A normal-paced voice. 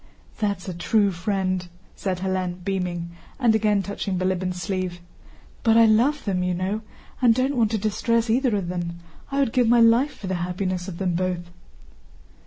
Yes: average, 180 wpm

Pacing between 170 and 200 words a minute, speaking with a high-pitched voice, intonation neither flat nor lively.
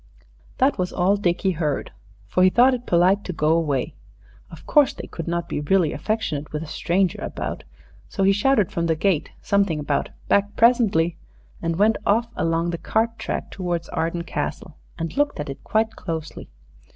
No: average, 180 wpm; medium, 180 Hz; average, 4.1 semitones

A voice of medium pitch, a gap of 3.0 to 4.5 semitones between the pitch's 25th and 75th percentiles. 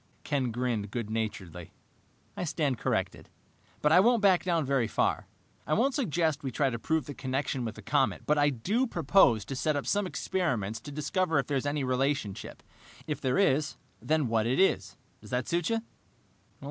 No: medium, 145 Hz; wide, 5.4 semitones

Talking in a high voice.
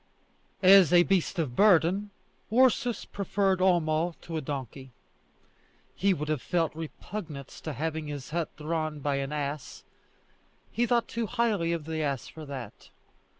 No: medium, 160 Hz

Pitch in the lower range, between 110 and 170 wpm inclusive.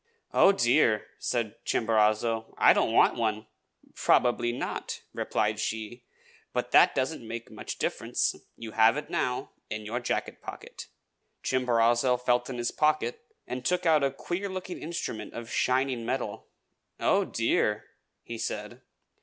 Yes: low, 120 Hz; average, 140 wpm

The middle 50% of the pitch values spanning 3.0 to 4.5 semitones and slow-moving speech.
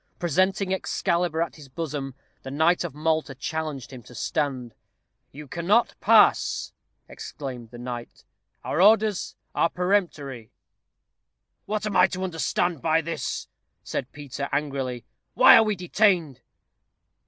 No: average, 5.0 semitones; slow, 130 wpm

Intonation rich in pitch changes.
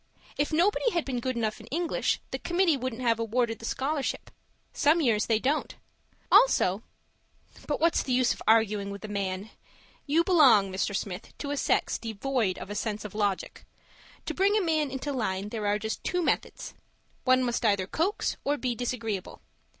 Yes: wide, 5.8 semitones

